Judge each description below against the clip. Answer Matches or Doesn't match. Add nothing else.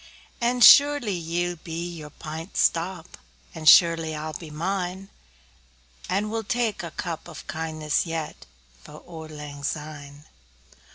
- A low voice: Doesn't match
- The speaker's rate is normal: Doesn't match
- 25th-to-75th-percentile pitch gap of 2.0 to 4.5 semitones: Matches